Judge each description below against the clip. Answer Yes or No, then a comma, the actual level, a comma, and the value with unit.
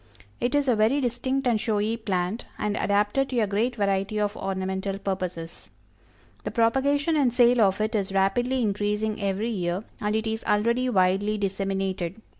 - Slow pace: No, average, 165 wpm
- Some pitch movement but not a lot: Yes, average, 3.5 semitones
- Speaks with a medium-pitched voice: No, high, 210 Hz